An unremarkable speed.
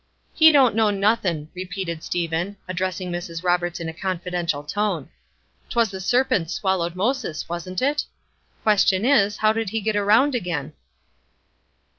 Yes: average, 145 wpm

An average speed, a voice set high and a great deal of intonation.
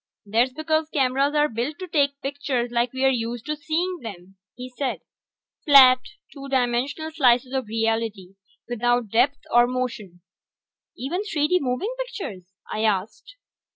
No: average, 145 wpm; very high, 255 Hz; average, 4.1 semitones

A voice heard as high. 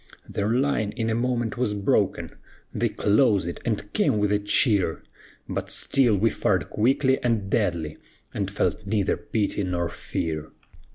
No: low, 105 Hz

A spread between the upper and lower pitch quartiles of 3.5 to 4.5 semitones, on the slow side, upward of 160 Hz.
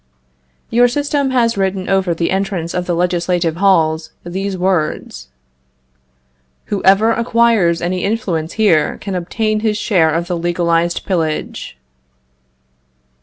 Yes: average, 3.8 semitones; slow, 120 wpm; medium, 185 Hz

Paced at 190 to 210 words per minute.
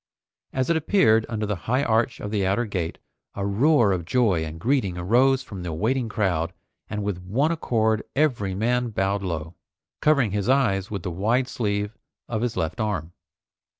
No: average, 180 wpm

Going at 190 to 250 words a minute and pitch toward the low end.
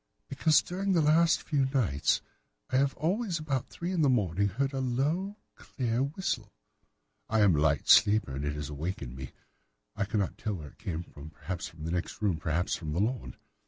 Yes: average, 195 wpm; low, 110 Hz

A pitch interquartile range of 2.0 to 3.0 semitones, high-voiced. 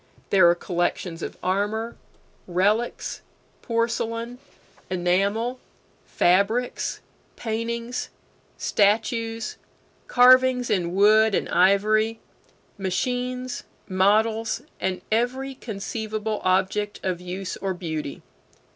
No: average, 3.6 semitones; high, 215 Hz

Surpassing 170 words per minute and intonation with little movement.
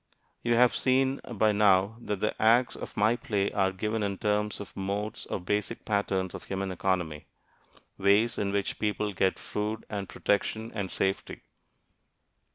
No: average, 160 wpm; narrow, 2.1 semitones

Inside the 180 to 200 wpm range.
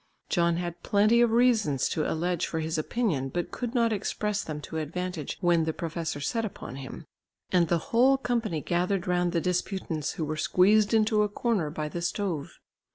Yes: average, 185 wpm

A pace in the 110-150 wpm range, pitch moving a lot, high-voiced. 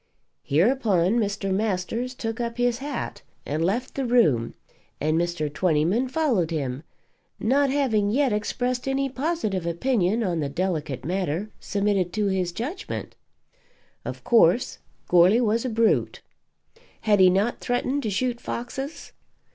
Yes: slow, 135 wpm; wide, 5.8 semitones; high, 215 Hz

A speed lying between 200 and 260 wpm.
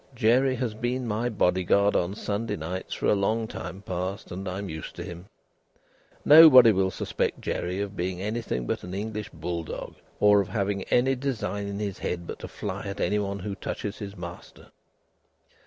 No: average, 185 wpm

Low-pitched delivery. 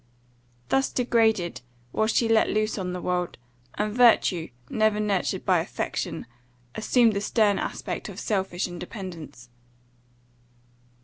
No: high, 210 Hz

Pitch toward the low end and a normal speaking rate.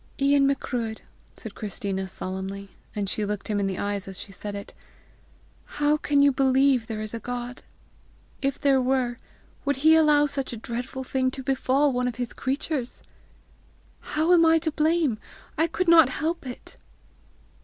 No: very high, 260 Hz; average, 170 wpm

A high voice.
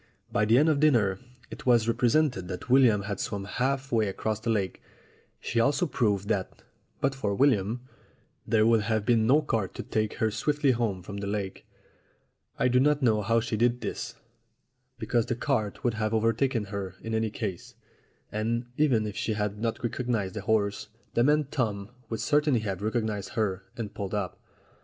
No: low, 110 Hz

